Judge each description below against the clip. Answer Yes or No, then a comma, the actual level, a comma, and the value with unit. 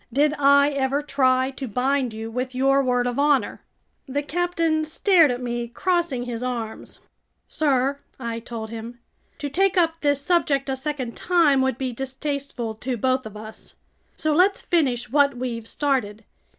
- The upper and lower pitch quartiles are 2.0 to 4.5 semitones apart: Yes, average, 3.1 semitones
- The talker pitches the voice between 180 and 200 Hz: No, very high, 265 Hz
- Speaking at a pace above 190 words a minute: No, average, 165 wpm